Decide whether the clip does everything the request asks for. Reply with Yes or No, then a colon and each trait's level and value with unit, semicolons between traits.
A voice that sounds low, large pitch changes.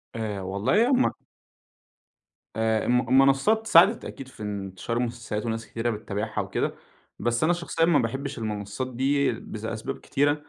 No: low, 120 Hz; average, 4.3 semitones